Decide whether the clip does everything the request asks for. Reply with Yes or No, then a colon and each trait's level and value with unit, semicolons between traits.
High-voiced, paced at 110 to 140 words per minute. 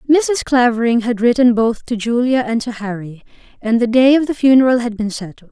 No: high, 235 Hz; fast, 205 wpm